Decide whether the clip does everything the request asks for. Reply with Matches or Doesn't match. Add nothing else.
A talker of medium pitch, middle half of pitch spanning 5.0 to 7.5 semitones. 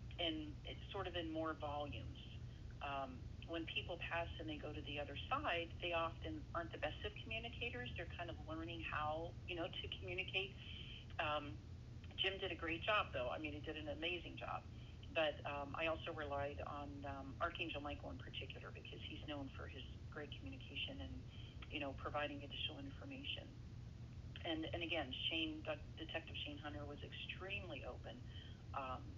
Doesn't match